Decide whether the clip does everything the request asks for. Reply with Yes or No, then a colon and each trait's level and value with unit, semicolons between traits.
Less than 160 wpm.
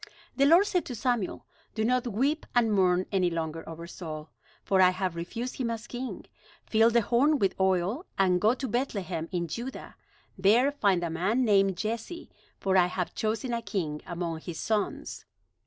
No: average, 180 wpm